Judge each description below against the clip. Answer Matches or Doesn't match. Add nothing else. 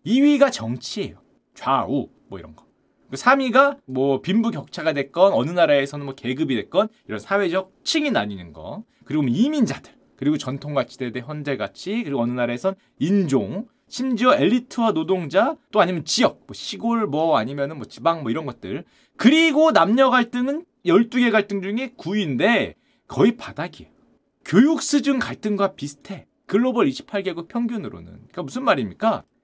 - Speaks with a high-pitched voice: Matches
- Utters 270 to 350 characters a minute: Matches